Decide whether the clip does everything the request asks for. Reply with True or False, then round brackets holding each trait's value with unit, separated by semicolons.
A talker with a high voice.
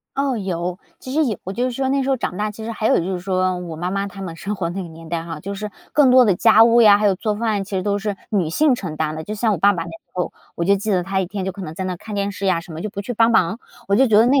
True (200 Hz)